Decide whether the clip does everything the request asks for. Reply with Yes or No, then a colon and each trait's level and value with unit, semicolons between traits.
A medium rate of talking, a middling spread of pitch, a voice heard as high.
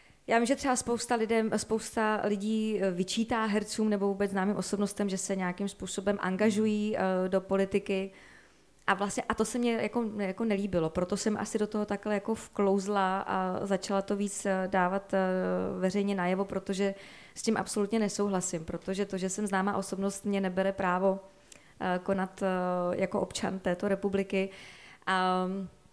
No: average, 160 wpm; narrow, 1.8 semitones; high, 195 Hz